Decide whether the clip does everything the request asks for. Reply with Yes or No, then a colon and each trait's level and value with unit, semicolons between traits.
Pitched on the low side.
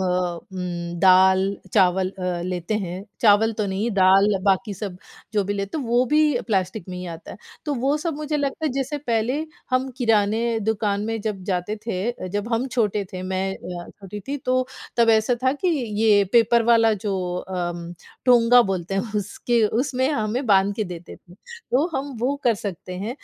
No: high, 210 Hz